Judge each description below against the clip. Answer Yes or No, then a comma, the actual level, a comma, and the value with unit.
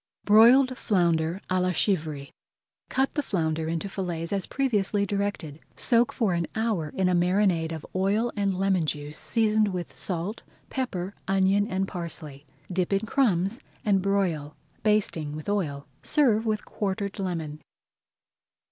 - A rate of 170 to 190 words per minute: No, average, 140 wpm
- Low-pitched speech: No, high, 190 Hz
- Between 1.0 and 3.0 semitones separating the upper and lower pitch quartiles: No, average, 4.0 semitones